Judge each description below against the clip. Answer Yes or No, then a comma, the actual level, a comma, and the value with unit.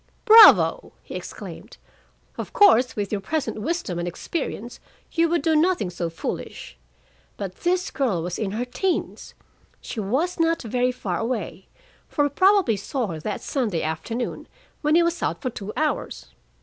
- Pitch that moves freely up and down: Yes, wide, 8.7 semitones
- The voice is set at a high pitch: Yes, very high, 250 Hz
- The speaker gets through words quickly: No, average, 160 wpm